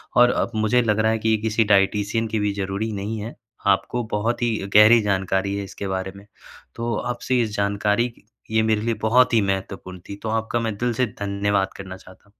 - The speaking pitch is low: Yes, low, 110 Hz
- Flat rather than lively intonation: Yes, narrow, 2.3 semitones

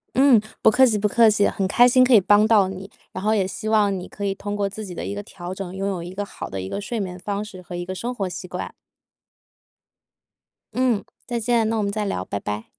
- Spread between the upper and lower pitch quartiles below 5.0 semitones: Yes, average, 2.7 semitones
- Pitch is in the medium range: No, high, 200 Hz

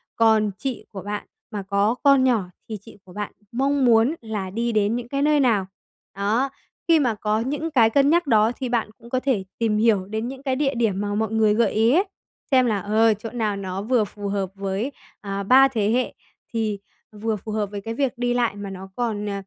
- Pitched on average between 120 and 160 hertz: No, high, 225 Hz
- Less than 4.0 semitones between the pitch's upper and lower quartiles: Yes, average, 3.5 semitones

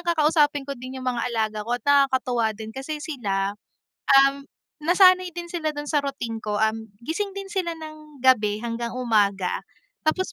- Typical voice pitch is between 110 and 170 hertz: No, very high, 275 Hz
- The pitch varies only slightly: No, average, 5.3 semitones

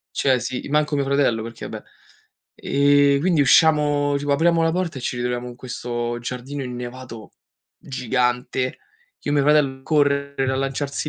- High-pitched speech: No, low, 135 Hz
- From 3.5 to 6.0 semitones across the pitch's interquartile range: No, average, 2.7 semitones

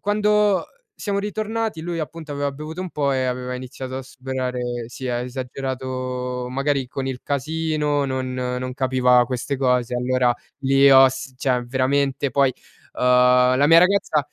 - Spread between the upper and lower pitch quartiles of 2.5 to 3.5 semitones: Yes, average, 2.9 semitones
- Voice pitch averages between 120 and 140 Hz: Yes, low, 135 Hz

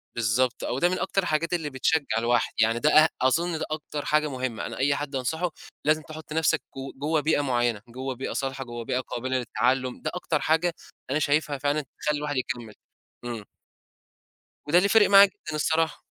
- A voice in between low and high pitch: Yes, medium, 145 Hz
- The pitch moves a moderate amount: Yes, average, 3.8 semitones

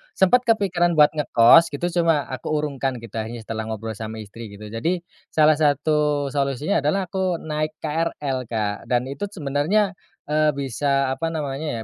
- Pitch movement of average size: Yes, average, 4.9 semitones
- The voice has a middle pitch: Yes, medium, 145 Hz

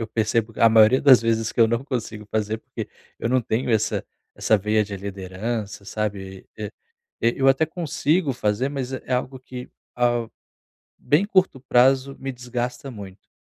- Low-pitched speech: Yes, low, 115 Hz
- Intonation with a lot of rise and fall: No, average, 3.5 semitones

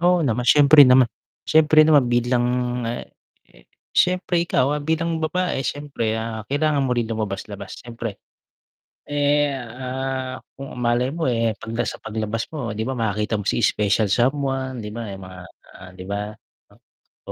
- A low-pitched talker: Yes, low, 125 Hz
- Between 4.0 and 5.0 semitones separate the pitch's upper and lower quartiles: Yes, average, 4.6 semitones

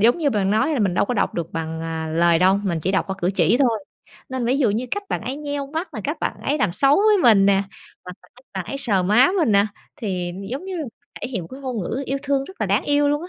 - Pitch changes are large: Yes, wide, 6.6 semitones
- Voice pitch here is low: No, high, 230 Hz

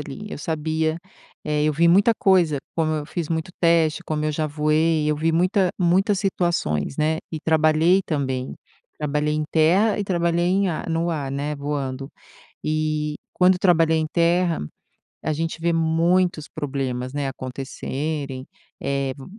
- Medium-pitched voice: Yes, medium, 155 Hz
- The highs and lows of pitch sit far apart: No, narrow, 2.5 semitones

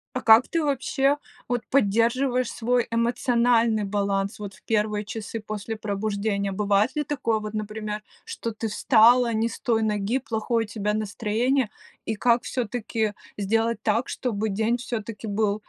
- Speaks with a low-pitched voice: No, high, 220 Hz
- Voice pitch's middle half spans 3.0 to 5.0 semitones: No, narrow, 2.4 semitones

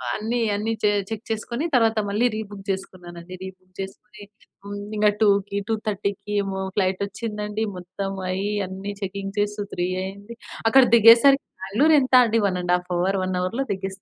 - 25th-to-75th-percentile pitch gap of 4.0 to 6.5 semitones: No, narrow, 2.4 semitones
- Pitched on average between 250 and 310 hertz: No, high, 200 Hz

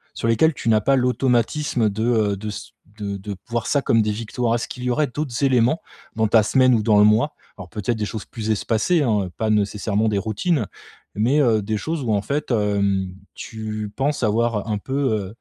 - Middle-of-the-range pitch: No, low, 110 Hz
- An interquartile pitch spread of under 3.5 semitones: Yes, average, 3.1 semitones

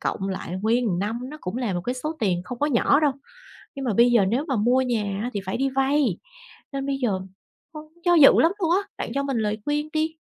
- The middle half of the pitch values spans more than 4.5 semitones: Yes, wide, 5.4 semitones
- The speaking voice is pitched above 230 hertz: Yes, very high, 250 Hz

